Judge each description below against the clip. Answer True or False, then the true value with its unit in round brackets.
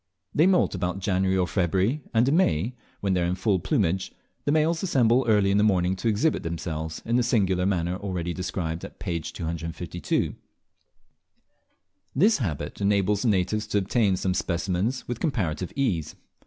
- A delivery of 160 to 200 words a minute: True (165 wpm)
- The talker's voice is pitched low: True (95 Hz)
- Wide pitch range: False (4.7 semitones)